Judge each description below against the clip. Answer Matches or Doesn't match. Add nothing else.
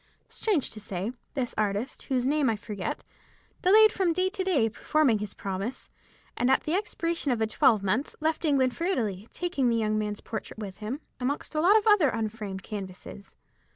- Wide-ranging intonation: Matches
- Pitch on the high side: Matches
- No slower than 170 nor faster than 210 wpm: Matches